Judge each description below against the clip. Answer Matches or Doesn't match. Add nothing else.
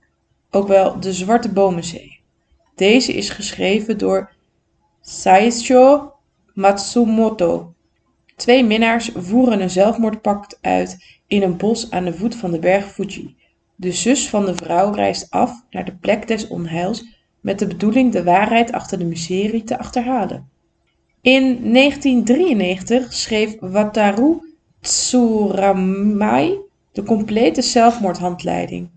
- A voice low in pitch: Doesn't match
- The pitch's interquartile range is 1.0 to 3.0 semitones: Doesn't match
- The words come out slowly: Matches